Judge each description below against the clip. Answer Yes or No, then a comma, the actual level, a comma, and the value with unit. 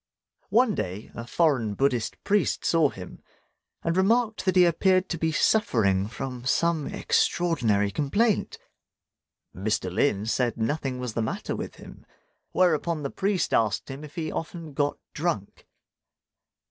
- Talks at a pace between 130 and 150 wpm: Yes, average, 140 wpm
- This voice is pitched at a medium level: Yes, medium, 145 Hz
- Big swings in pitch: Yes, wide, 7.3 semitones